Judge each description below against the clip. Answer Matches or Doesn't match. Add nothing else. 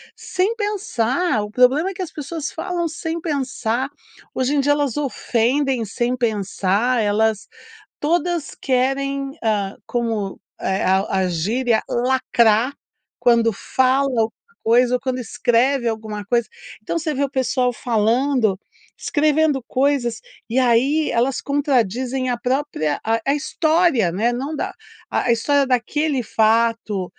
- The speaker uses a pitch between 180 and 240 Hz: Doesn't match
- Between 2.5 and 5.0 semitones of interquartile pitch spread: Matches